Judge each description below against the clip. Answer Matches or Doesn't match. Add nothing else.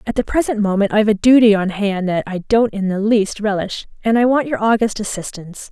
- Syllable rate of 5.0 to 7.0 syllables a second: Matches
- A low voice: Doesn't match